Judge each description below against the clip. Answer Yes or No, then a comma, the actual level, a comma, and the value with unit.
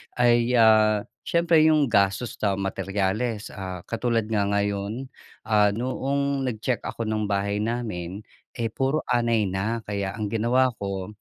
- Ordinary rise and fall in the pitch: Yes, average, 3.3 semitones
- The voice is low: Yes, low, 110 Hz